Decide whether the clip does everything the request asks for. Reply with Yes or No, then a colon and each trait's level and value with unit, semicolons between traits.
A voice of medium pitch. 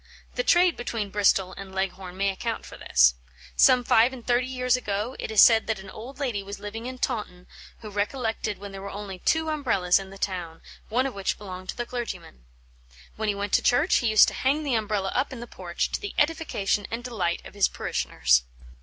No: high, 210 Hz